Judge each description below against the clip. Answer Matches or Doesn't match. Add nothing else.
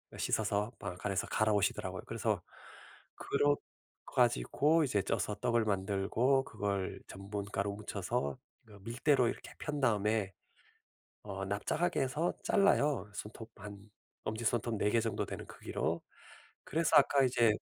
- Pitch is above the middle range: Doesn't match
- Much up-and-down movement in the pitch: Doesn't match